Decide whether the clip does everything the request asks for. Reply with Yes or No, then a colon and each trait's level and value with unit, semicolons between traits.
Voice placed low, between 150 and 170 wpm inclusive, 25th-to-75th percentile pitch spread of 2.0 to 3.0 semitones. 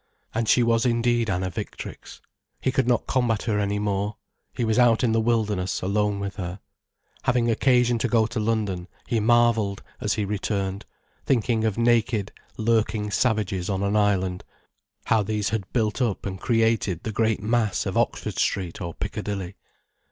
Yes: low, 110 Hz; average, 165 wpm; average, 2.7 semitones